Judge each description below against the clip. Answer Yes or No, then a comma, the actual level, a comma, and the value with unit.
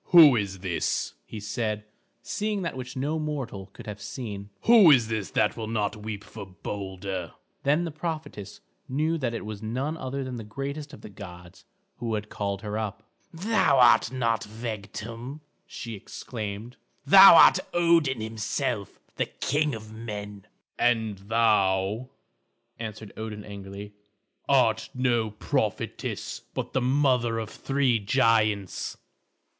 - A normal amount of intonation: Yes, average, 4.5 semitones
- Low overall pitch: Yes, low, 115 Hz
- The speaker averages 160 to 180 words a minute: No, average, 140 wpm